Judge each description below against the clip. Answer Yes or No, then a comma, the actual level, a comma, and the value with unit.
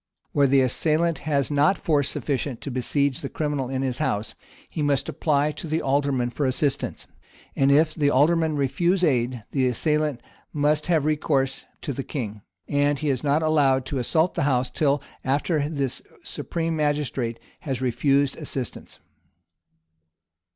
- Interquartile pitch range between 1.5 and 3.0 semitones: Yes, narrow, 2.4 semitones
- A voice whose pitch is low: No, medium, 145 Hz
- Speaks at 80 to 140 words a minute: No, average, 155 wpm